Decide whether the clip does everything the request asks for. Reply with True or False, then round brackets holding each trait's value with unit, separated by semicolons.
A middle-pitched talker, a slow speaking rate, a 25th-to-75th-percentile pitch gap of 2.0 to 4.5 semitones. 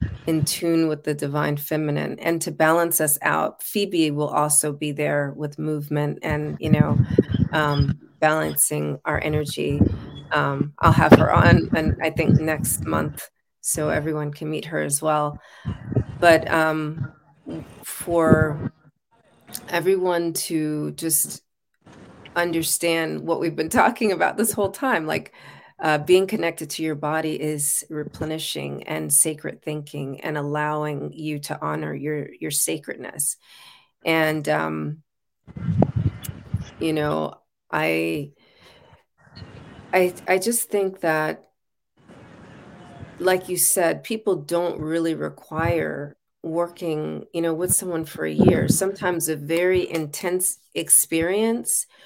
True (155 Hz; 125 wpm; 2.4 semitones)